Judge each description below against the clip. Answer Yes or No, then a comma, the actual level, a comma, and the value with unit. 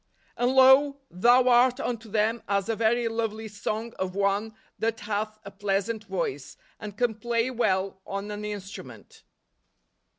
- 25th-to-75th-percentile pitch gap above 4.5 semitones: No, average, 2.8 semitones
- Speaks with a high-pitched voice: Yes, high, 220 Hz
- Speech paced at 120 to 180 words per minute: Yes, average, 145 wpm